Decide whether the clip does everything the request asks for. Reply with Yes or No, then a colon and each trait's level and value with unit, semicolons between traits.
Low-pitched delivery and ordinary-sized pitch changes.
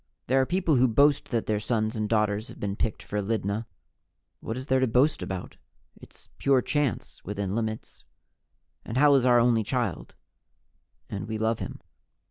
Yes: low, 115 Hz; average, 3.5 semitones